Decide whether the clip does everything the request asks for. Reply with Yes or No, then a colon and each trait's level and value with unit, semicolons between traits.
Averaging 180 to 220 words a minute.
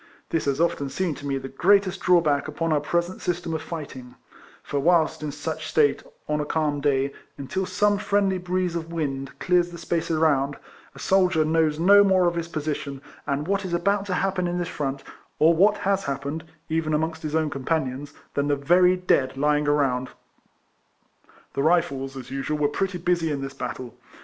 Yes: average, 190 wpm